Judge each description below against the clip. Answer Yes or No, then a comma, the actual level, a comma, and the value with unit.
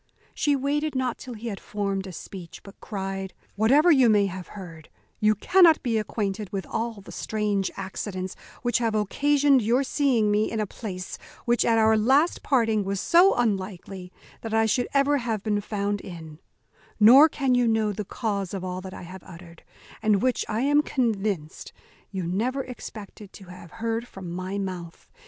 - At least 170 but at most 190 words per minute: Yes, average, 180 wpm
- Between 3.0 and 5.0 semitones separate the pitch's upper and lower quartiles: Yes, average, 4.0 semitones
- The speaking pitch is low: No, high, 215 Hz